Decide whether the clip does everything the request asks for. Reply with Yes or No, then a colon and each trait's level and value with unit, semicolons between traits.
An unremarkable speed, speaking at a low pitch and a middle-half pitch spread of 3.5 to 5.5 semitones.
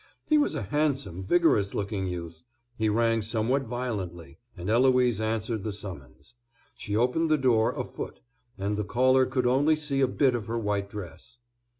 Yes: average, 175 wpm; low, 115 Hz; average, 4.3 semitones